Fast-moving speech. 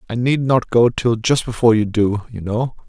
Yes: fast, 230 wpm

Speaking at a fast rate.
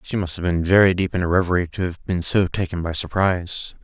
Yes: fast, 250 wpm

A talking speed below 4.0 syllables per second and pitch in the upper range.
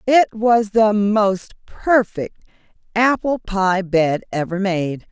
Yes: 3.2 syllables/s; high, 205 Hz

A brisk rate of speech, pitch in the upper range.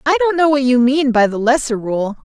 Yes: fast, 260 wpm; very high, 260 Hz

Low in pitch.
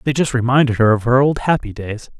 Yes: low, 125 Hz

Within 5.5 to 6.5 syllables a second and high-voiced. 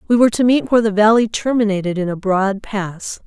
Yes: 5.9 syllables/s; high, 210 Hz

